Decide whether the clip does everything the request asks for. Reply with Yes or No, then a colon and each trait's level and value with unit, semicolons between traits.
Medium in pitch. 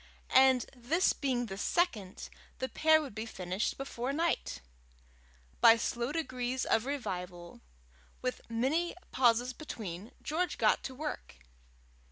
No: very high, 250 Hz